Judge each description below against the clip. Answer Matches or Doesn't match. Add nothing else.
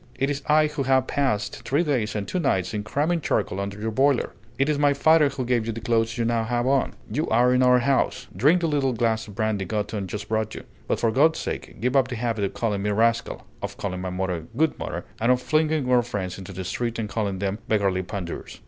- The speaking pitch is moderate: Doesn't match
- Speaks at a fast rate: Matches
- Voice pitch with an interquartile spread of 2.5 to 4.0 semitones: Doesn't match